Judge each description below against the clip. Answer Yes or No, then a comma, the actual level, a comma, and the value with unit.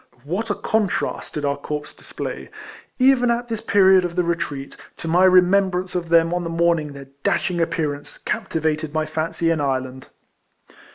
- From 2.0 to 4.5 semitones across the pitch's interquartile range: Yes, average, 3.7 semitones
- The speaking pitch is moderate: Yes, medium, 170 Hz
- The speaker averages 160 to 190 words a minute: Yes, average, 165 wpm